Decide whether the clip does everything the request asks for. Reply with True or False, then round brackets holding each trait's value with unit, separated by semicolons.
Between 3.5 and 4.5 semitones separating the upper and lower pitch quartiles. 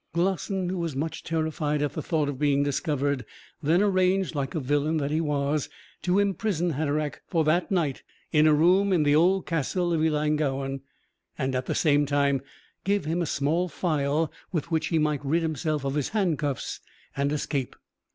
False (3.1 semitones)